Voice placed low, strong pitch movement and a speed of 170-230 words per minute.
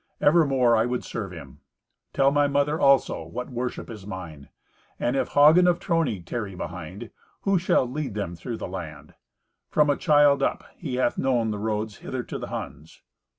Yes: low, 120 Hz; wide, 6.5 semitones; average, 180 wpm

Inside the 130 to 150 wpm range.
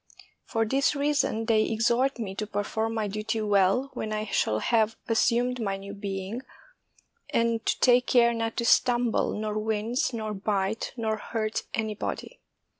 No: average, 160 wpm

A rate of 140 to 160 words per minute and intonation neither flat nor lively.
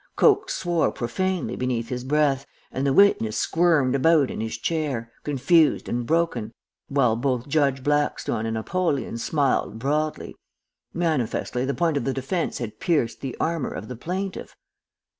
Yes: average, 150 wpm; average, 5.0 semitones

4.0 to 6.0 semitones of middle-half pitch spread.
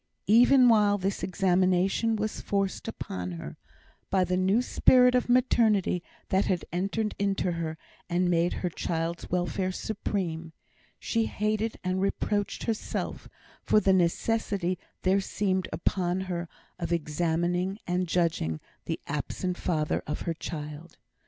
No: average, 3.1 semitones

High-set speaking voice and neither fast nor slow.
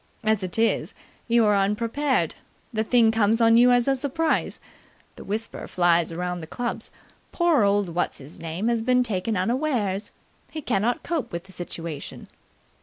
Yes: high, 220 Hz; average, 165 wpm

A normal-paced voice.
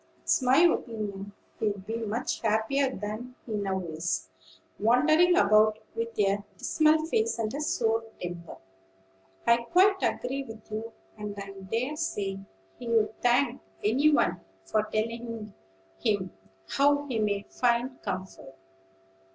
No: slow, 130 wpm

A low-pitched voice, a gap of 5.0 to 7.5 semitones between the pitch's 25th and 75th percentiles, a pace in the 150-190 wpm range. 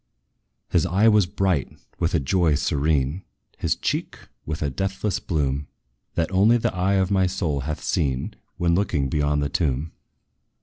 No: very low, 85 Hz; average, 4.6 semitones; average, 160 wpm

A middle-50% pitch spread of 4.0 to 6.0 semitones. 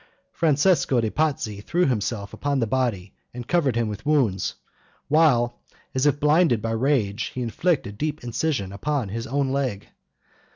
Yes: average, 5.0 semitones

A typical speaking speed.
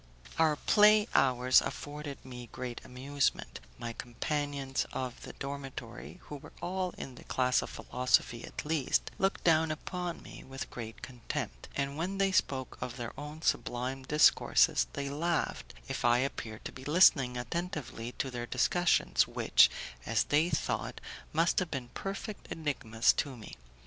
Yes: average, 155 wpm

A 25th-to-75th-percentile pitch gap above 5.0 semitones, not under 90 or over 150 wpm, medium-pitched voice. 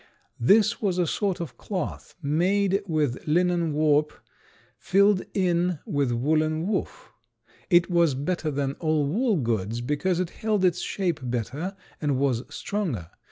No: average, 4.5 semitones; average, 140 wpm; medium, 165 Hz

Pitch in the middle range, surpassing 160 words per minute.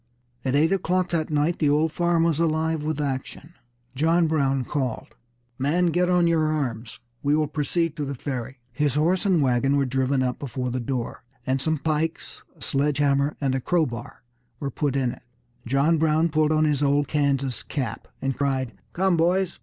Yes: medium, 145 Hz; average, 185 wpm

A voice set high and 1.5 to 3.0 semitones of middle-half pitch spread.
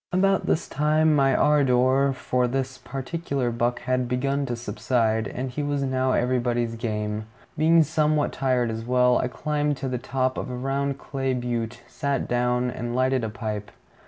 No: low, 130 Hz; narrow, 2.4 semitones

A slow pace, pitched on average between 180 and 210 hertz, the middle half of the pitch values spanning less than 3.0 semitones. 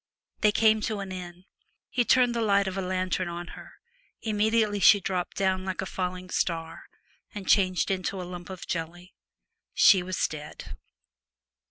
No: average, 165 wpm; medium, 185 Hz; narrow, 2.4 semitones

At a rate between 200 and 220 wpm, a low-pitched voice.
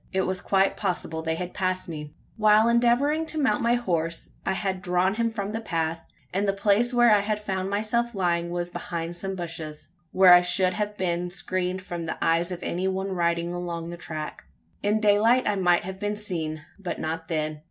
No: fast, 205 wpm; medium, 185 Hz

